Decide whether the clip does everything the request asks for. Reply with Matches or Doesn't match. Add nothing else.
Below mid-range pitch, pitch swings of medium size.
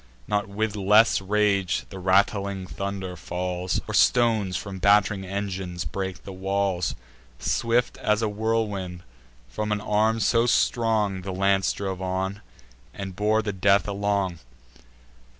Doesn't match